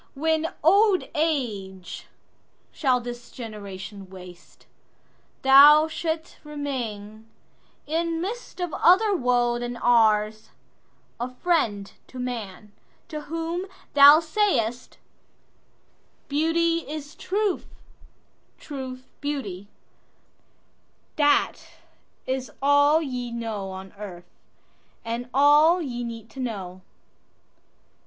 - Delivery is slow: Yes, slow, 80 wpm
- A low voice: No, very high, 255 Hz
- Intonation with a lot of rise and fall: Yes, wide, 6.3 semitones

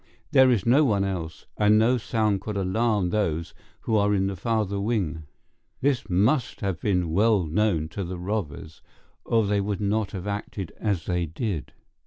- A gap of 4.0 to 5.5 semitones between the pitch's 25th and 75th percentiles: No, average, 3.5 semitones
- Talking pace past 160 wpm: Yes, average, 175 wpm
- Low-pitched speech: Yes, low, 100 Hz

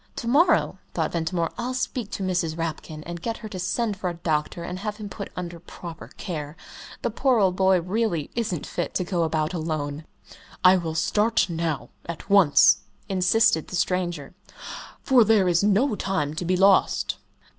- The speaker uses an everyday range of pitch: Yes, average, 4.1 semitones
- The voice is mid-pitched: Yes, medium, 180 Hz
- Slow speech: No, average, 175 wpm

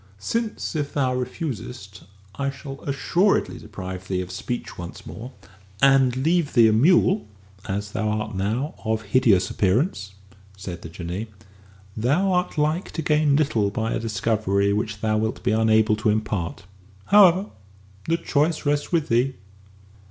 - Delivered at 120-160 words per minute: Yes, average, 150 wpm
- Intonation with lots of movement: Yes, wide, 6.4 semitones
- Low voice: Yes, low, 115 Hz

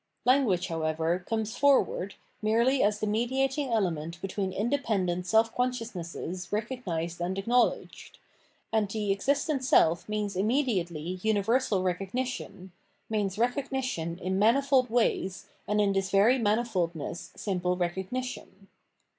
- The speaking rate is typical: No, slow, 120 wpm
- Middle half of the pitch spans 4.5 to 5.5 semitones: Yes, average, 5.1 semitones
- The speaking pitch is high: Yes, high, 205 Hz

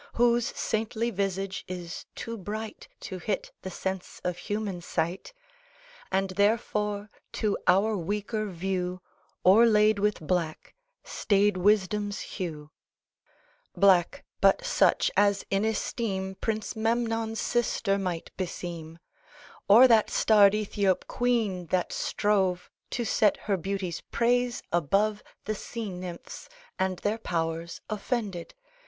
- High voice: Yes, high, 200 Hz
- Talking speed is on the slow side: Yes, slow, 115 wpm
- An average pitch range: Yes, average, 3.0 semitones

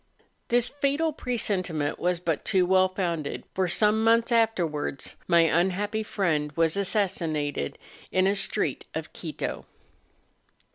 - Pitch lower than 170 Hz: No, medium, 185 Hz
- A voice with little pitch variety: No, average, 4.8 semitones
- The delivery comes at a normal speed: No, slow, 125 wpm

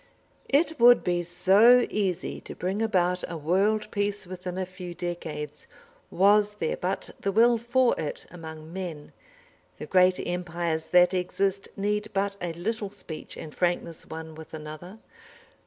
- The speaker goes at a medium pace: Yes, average, 150 wpm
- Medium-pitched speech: Yes, medium, 180 Hz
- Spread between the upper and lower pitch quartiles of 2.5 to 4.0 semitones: Yes, average, 3.2 semitones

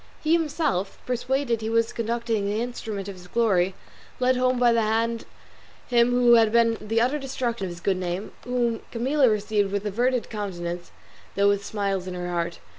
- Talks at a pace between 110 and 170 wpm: No, average, 185 wpm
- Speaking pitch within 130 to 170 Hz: No, high, 225 Hz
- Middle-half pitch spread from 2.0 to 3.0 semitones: No, average, 3.6 semitones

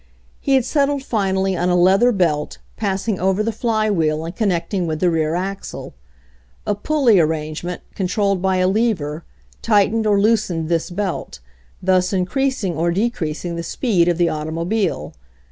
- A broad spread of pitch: No, average, 4.2 semitones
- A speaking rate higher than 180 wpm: No, average, 160 wpm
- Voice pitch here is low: No, high, 190 Hz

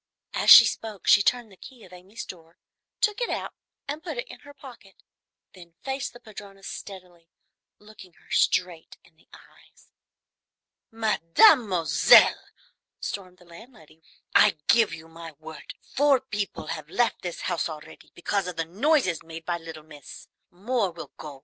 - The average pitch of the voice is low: No, medium, 185 Hz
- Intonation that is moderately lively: No, wide, 5.7 semitones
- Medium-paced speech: Yes, average, 160 wpm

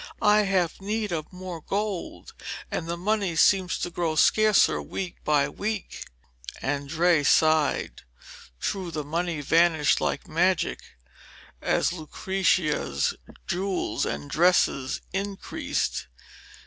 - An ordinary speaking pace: No, slow, 110 wpm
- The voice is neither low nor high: Yes, medium, 175 Hz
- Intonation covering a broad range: No, average, 3.7 semitones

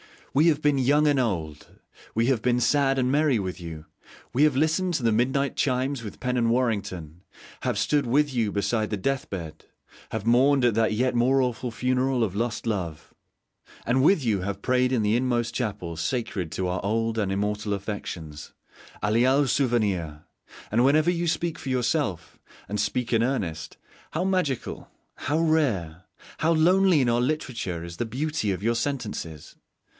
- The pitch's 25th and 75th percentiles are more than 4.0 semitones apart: Yes, average, 5.1 semitones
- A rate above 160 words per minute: Yes, average, 180 wpm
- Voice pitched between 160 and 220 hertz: No, low, 120 Hz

